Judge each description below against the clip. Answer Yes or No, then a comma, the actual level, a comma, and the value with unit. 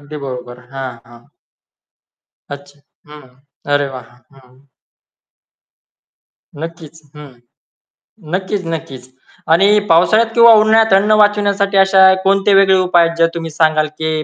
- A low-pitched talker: No, medium, 165 Hz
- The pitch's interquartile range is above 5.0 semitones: Yes, wide, 5.4 semitones